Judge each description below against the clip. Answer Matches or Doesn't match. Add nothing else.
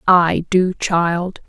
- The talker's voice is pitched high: Doesn't match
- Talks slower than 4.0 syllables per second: Matches